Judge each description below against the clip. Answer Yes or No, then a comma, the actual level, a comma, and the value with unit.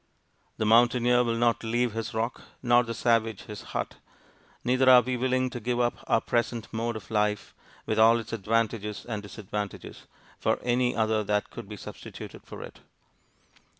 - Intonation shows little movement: Yes, narrow, 2.0 semitones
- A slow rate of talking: No, average, 170 wpm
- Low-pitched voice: Yes, low, 115 Hz